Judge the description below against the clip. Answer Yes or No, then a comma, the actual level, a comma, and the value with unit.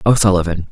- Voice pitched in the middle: No, very low, 95 Hz